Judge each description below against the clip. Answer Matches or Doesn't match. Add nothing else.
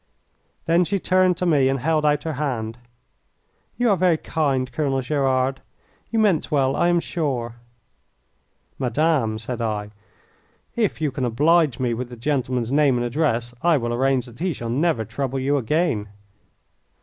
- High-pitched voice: Doesn't match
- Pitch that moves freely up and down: Doesn't match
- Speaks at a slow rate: Doesn't match